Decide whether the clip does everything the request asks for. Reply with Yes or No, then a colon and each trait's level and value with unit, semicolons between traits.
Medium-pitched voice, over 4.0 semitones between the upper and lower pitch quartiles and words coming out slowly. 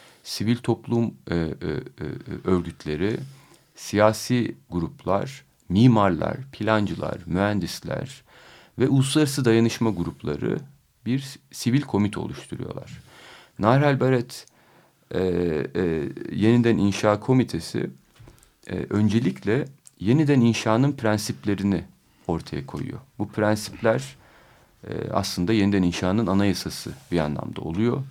No: low, 110 Hz; average, 4.6 semitones; slow, 90 wpm